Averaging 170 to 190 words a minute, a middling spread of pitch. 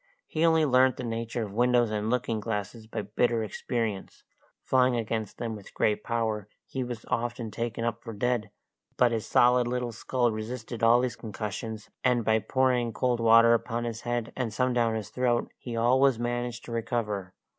No: average, 180 wpm; narrow, 1.8 semitones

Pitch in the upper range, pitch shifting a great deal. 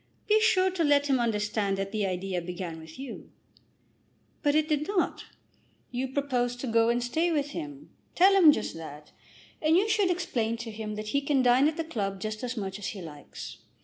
Yes: high, 245 Hz; wide, 6.6 semitones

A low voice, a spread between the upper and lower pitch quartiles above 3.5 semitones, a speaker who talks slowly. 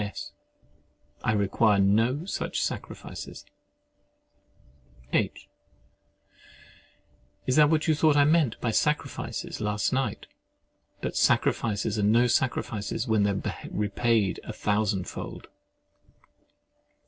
Yes: low, 110 Hz; average, 4.3 semitones; slow, 105 wpm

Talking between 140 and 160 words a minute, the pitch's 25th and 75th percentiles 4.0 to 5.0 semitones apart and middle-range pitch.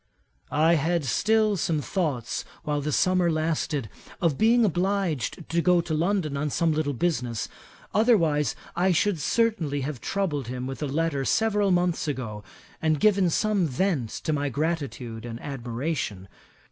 Yes: average, 150 wpm; average, 4.7 semitones; medium, 155 Hz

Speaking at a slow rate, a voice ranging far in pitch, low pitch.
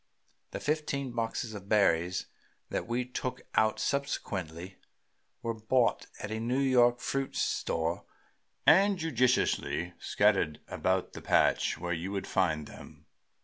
Yes: slow, 130 wpm; wide, 5.8 semitones; low, 110 Hz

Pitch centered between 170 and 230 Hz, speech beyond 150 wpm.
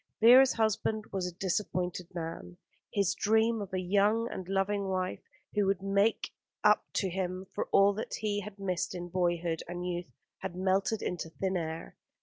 Yes: high, 190 Hz; average, 170 wpm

